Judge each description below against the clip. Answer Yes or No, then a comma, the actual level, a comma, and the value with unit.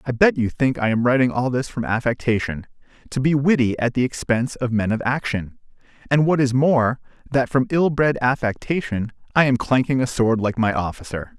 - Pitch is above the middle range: No, low, 125 Hz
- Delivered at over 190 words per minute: Yes, average, 200 wpm